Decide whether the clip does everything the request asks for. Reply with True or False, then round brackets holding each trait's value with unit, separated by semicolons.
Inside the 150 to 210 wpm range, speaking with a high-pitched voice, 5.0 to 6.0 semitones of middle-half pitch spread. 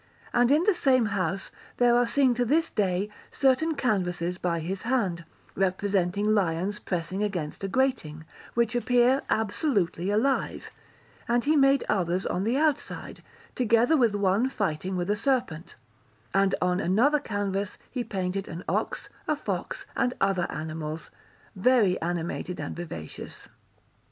False (140 wpm; 205 Hz; 5.5 semitones)